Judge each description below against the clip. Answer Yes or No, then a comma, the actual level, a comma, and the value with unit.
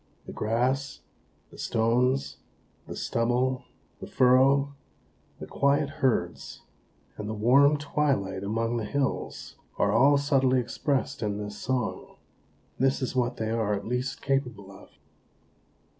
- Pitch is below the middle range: Yes, low, 125 Hz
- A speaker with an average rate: No, slow, 130 wpm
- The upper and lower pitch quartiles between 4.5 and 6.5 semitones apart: No, average, 3.4 semitones